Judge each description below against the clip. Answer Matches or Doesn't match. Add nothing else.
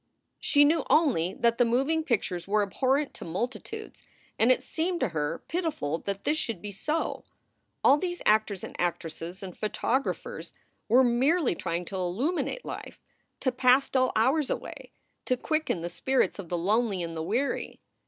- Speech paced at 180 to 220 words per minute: Doesn't match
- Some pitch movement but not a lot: Doesn't match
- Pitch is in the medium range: Doesn't match